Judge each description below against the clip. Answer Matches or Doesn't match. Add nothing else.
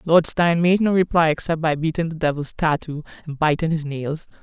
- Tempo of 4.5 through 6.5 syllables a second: Matches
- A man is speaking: Doesn't match